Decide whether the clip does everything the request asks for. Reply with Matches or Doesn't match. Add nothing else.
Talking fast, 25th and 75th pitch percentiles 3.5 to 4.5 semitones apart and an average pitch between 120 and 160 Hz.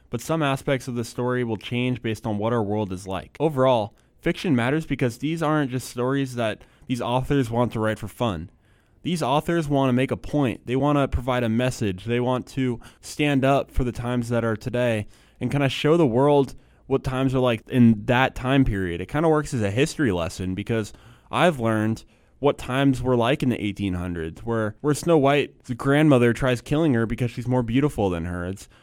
Matches